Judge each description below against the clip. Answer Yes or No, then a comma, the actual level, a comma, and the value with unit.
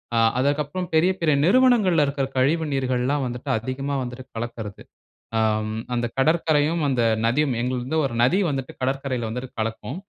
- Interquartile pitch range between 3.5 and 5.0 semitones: Yes, average, 3.8 semitones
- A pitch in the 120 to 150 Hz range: Yes, low, 135 Hz